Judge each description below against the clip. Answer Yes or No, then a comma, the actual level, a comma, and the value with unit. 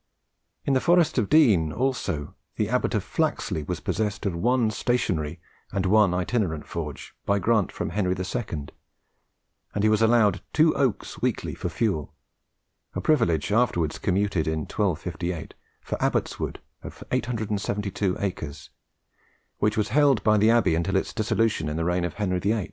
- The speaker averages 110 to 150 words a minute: No, average, 160 wpm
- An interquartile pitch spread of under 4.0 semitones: No, average, 4.5 semitones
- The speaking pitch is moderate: No, low, 100 Hz